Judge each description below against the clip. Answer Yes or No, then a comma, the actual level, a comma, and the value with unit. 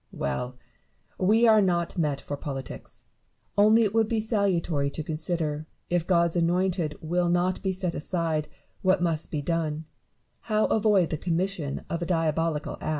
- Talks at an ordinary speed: Yes, average, 160 wpm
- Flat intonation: No, average, 3.4 semitones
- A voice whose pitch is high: No, medium, 170 Hz